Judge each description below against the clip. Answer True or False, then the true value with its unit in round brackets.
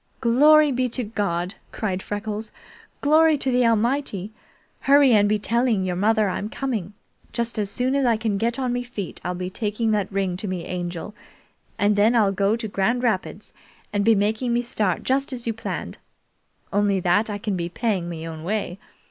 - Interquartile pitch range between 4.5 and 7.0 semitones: False (3.5 semitones)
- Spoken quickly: False (190 wpm)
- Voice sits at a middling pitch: False (215 Hz)